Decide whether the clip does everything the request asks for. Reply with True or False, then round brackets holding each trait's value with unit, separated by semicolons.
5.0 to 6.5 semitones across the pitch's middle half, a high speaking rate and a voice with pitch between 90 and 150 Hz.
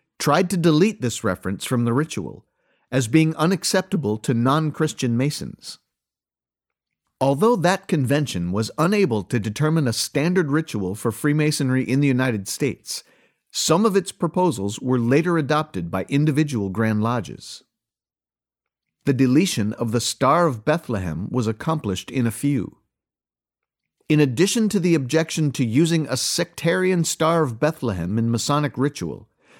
False (5.6 semitones; 140 wpm; 140 Hz)